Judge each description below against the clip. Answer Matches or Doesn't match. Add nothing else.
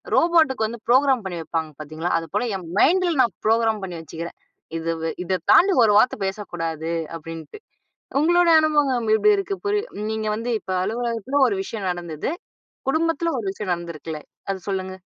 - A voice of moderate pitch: Doesn't match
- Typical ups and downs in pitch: Doesn't match